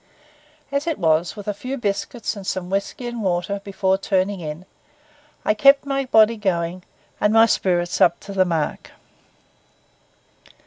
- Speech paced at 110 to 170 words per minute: Yes, average, 150 wpm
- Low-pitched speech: No, high, 200 Hz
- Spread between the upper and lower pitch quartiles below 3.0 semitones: No, average, 3.9 semitones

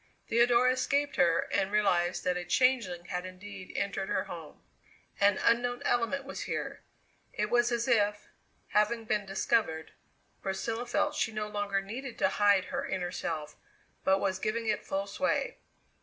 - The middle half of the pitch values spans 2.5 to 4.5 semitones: Yes, average, 3.7 semitones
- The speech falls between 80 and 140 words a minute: No, average, 155 wpm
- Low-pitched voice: No, high, 210 Hz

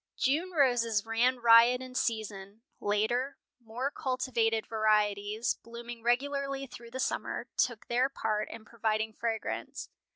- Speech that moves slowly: Yes, slow, 125 wpm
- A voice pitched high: Yes, high, 235 Hz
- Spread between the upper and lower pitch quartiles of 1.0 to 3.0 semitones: Yes, narrow, 2.6 semitones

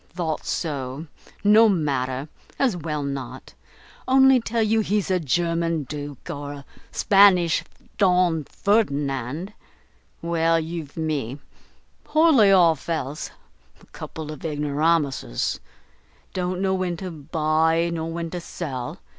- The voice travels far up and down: No, average, 4.1 semitones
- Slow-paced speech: Yes, slow, 120 wpm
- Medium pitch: Yes, medium, 165 Hz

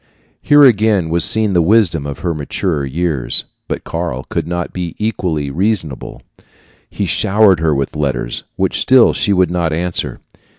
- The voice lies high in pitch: No, very low, 85 Hz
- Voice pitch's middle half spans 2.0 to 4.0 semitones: No, average, 4.7 semitones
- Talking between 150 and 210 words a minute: Yes, average, 160 wpm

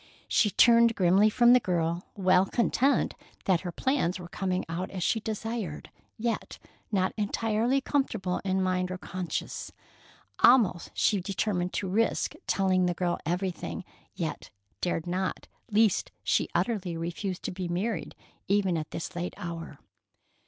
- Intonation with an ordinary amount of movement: Yes, average, 3.6 semitones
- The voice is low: No, medium, 185 Hz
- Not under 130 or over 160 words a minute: Yes, average, 145 wpm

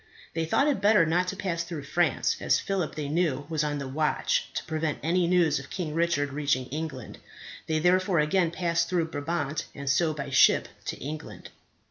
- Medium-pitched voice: Yes, medium, 160 Hz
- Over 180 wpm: Yes, average, 190 wpm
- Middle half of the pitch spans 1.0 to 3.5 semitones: Yes, average, 3.1 semitones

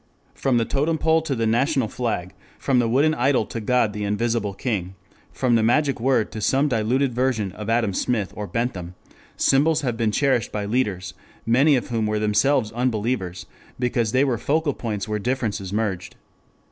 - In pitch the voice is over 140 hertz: No, low, 115 Hz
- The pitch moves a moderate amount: Yes, average, 3.8 semitones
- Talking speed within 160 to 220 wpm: Yes, average, 180 wpm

